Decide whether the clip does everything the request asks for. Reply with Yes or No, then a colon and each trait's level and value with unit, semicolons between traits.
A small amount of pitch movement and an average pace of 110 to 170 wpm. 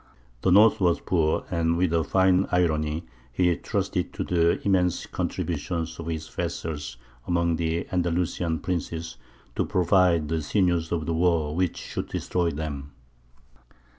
Yes: narrow, 2.0 semitones; average, 140 wpm